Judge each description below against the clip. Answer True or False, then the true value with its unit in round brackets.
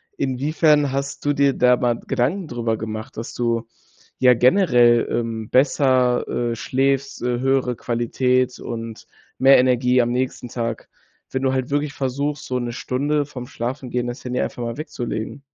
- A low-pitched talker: True (125 Hz)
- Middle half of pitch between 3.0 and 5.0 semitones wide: False (2.4 semitones)